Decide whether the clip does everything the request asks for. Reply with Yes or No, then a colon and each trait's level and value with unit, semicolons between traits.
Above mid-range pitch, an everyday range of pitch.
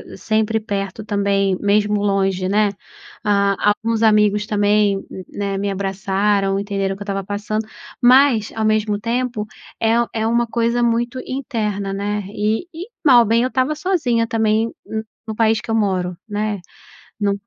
No: high, 210 Hz; narrow, 2.3 semitones